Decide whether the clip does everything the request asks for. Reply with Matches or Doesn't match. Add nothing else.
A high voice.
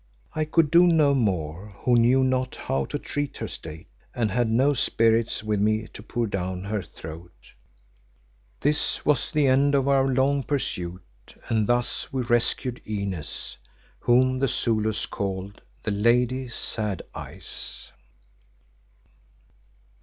Doesn't match